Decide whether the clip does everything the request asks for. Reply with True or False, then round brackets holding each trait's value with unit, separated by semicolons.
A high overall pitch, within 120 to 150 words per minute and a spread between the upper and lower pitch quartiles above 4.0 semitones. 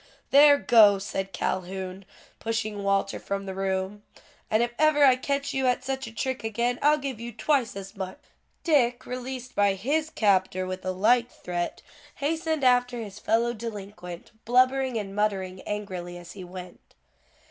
False (215 Hz; 160 wpm; 4.8 semitones)